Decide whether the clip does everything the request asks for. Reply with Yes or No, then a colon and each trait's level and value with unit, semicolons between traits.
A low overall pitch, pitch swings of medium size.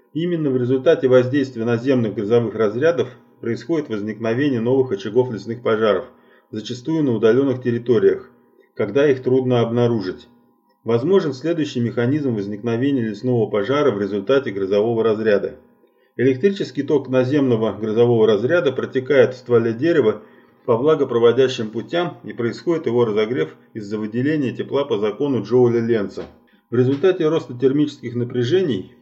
Yes: low, 125 Hz; average, 3.4 semitones